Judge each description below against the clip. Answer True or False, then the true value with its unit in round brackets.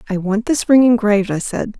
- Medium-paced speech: False (235 wpm)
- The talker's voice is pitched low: False (220 Hz)